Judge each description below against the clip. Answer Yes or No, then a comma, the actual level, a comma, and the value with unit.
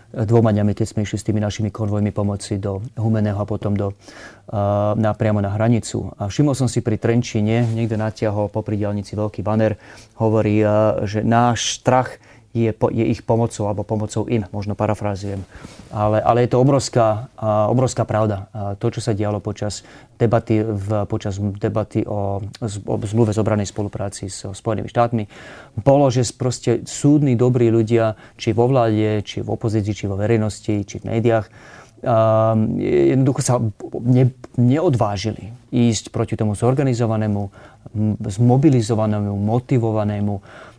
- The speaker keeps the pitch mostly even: Yes, narrow, 2.1 semitones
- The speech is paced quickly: No, average, 150 wpm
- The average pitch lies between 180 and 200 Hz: No, low, 110 Hz